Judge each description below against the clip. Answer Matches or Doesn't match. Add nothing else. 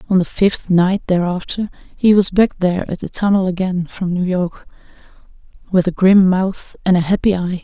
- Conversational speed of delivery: Matches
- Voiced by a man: Doesn't match